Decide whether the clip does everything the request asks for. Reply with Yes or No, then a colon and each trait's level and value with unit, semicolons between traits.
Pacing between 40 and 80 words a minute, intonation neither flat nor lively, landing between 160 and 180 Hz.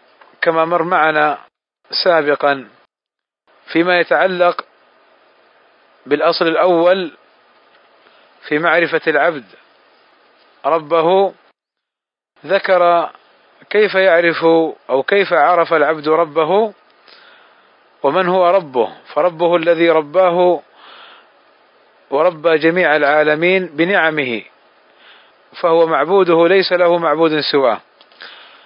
No: average, 75 wpm; narrow, 2.3 semitones; medium, 170 Hz